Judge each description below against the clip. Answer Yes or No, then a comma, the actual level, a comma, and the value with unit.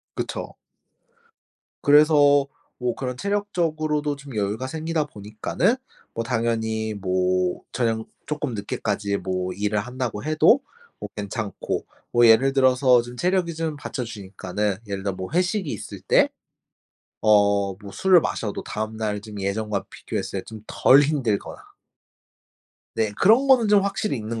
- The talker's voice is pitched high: No, low, 115 Hz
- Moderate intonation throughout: No, wide, 6.6 semitones